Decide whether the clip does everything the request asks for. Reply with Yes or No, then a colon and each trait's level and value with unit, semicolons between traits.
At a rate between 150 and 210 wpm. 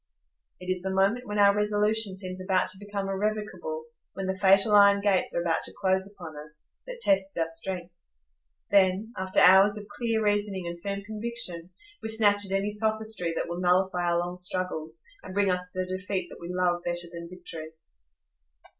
Yes: average, 180 wpm